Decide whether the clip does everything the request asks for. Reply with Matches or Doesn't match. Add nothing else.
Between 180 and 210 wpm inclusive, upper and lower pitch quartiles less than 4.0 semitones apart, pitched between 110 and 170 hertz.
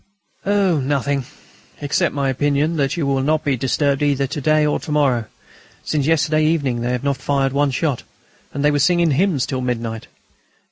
Matches